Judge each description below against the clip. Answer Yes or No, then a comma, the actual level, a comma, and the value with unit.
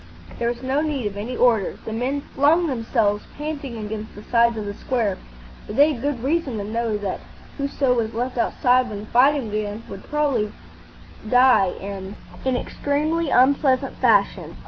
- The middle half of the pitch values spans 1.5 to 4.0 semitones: No, average, 4.6 semitones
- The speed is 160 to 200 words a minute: Yes, average, 175 wpm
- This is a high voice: Yes, high, 245 Hz